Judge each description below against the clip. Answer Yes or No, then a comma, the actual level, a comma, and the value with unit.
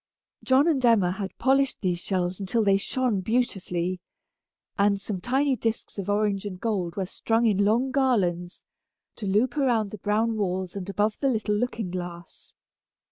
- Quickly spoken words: No, average, 165 wpm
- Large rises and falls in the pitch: No, average, 3.9 semitones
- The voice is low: No, high, 205 Hz